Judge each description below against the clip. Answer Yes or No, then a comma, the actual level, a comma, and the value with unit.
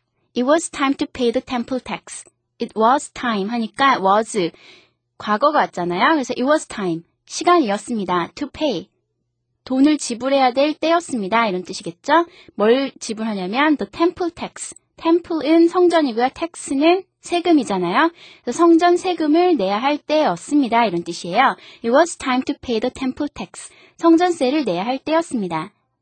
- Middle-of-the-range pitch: No, very high, 265 Hz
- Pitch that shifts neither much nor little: No, wide, 7.2 semitones